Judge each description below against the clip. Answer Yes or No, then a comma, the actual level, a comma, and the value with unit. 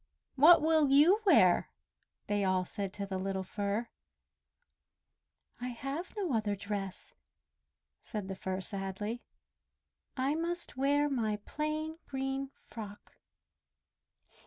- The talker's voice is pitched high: Yes, high, 235 Hz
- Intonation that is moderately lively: No, wide, 6.7 semitones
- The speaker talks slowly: Yes, slow, 110 wpm